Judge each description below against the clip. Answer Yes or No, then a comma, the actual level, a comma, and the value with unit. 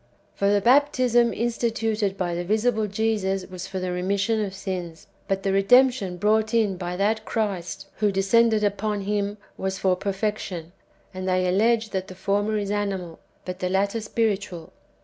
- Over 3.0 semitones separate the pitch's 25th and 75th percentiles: No, narrow, 2.6 semitones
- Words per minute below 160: No, average, 165 wpm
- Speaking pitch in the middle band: No, high, 200 Hz